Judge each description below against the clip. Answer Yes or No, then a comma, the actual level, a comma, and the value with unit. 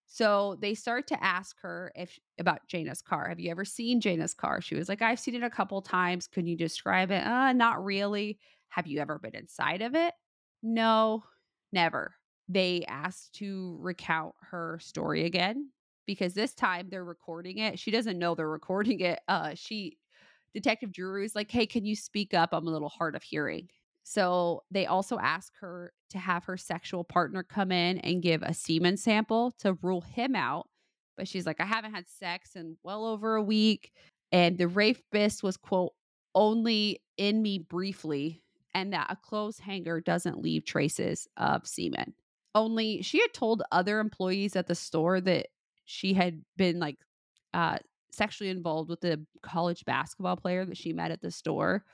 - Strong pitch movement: No, average, 3.8 semitones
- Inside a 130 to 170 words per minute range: No, average, 180 wpm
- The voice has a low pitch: No, high, 190 Hz